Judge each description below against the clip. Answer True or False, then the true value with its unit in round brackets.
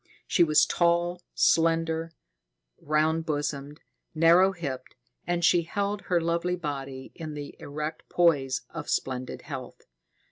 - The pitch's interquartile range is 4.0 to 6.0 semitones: False (2.9 semitones)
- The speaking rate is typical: False (120 wpm)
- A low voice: False (160 Hz)